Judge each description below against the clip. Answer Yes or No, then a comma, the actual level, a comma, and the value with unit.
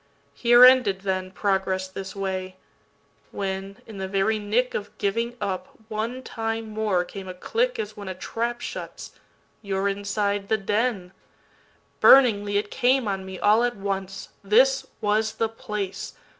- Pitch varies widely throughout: No, average, 2.7 semitones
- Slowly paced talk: Yes, slow, 130 wpm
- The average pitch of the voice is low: No, high, 205 Hz